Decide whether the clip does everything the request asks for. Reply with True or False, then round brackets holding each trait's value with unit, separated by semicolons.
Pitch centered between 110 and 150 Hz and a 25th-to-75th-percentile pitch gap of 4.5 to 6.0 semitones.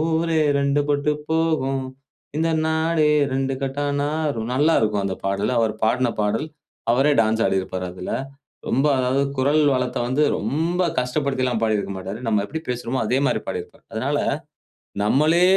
True (135 Hz; 5.1 semitones)